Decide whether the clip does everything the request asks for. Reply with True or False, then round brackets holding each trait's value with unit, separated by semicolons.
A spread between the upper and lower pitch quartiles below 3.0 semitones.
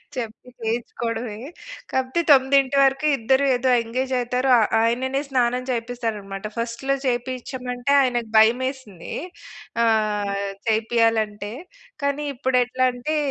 True (2.4 semitones)